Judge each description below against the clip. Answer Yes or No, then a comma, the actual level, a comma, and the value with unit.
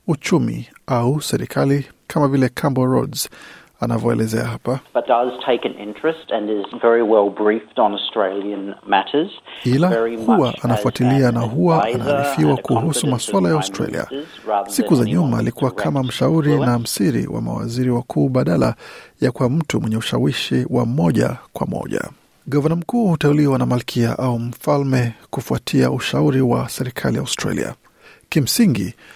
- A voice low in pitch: Yes, low, 125 Hz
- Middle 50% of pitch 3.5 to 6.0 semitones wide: Yes, average, 3.8 semitones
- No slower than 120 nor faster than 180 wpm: No, average, 110 wpm